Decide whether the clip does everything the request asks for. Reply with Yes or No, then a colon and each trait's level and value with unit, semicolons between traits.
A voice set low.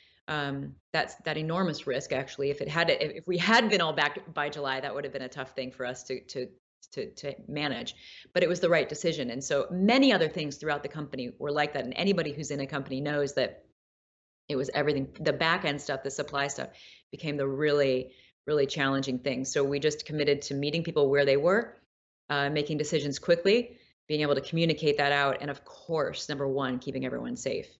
No: medium, 145 Hz